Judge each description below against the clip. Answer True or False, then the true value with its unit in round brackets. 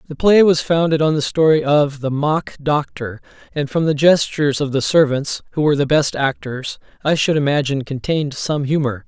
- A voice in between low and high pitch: True (145 Hz)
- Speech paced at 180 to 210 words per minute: True (190 wpm)